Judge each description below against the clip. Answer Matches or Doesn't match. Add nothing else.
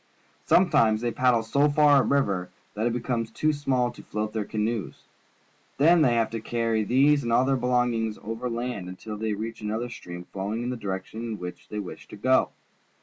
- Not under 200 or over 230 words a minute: Matches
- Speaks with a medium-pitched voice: Doesn't match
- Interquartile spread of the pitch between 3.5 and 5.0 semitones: Doesn't match